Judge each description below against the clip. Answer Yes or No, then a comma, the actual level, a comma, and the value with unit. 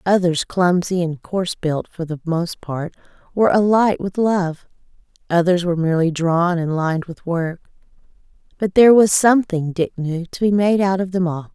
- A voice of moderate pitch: Yes, medium, 180 Hz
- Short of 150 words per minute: No, average, 175 wpm